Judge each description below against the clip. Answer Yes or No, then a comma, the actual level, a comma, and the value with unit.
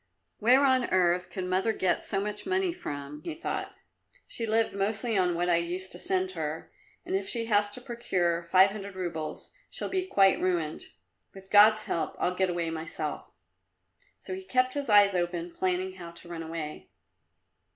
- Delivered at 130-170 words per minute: No, average, 180 wpm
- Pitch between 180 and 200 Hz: Yes, high, 190 Hz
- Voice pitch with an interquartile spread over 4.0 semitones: Yes, average, 5.0 semitones